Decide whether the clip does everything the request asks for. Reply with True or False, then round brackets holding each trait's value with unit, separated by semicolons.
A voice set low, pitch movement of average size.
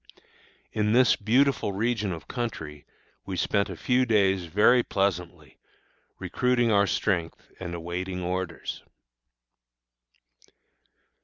True (100 Hz; 4.5 semitones)